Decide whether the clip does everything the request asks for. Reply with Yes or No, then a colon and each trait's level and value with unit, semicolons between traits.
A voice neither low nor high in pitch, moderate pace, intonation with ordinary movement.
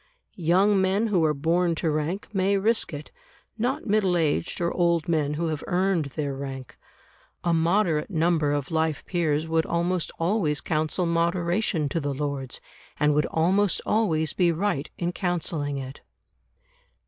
Yes: medium, 165 Hz; average, 155 wpm; average, 3.4 semitones